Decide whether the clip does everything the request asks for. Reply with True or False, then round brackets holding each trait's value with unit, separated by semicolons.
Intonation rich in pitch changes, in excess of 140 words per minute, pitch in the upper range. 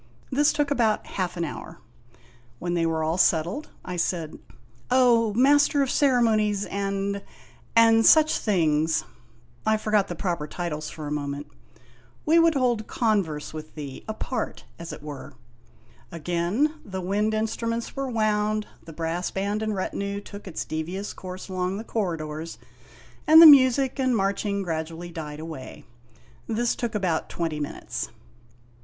True (5.7 semitones; 155 wpm; 195 Hz)